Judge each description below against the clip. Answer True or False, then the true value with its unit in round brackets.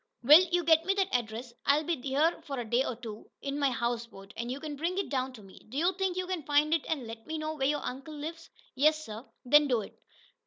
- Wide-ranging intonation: False (4.7 semitones)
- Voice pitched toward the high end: True (285 Hz)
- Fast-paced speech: True (250 wpm)